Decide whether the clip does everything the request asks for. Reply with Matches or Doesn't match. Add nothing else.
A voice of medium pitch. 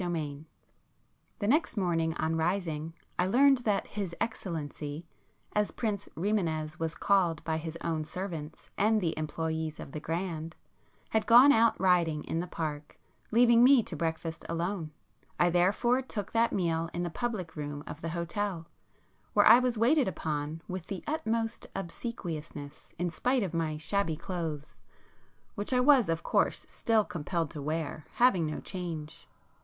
Matches